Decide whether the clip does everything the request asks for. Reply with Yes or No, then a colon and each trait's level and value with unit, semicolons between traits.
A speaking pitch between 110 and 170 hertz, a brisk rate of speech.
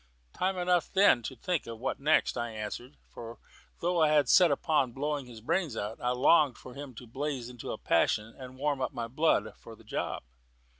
Yes: low, 135 Hz; fast, 210 wpm